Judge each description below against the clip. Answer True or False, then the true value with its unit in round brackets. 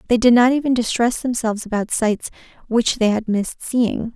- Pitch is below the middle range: False (230 Hz)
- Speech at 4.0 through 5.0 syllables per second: False (5.3 syllables/s)